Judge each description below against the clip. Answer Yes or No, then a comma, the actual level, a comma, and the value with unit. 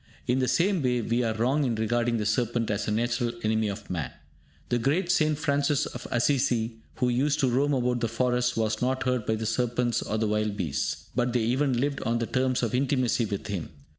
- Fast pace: Yes, fast, 215 wpm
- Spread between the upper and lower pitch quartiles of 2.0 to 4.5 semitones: Yes, average, 2.7 semitones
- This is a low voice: Yes, low, 120 Hz